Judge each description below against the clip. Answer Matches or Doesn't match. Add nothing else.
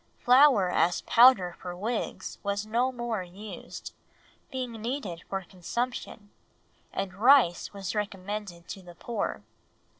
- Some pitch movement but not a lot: Matches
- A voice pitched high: Matches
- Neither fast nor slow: Doesn't match